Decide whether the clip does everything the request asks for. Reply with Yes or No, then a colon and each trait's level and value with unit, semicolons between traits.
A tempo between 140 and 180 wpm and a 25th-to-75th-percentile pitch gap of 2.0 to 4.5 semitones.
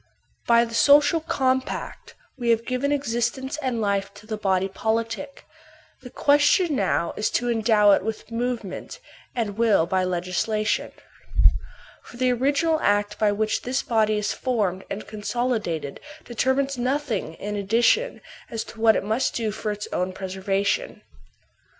Yes: average, 150 wpm; average, 3.7 semitones